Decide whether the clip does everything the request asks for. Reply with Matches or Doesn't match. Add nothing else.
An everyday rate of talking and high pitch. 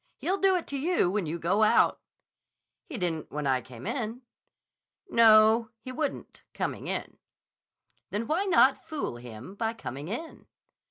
Matches